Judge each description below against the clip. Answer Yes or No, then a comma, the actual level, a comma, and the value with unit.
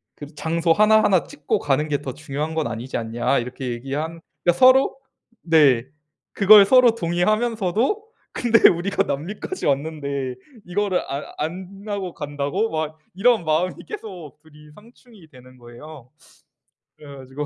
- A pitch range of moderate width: No, wide, 6.1 semitones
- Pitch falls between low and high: Yes, medium, 160 Hz